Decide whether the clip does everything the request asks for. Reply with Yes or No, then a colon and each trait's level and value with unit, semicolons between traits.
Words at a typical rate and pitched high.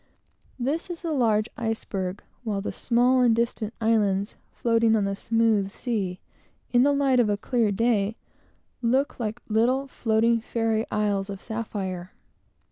Yes: average, 145 wpm; high, 225 Hz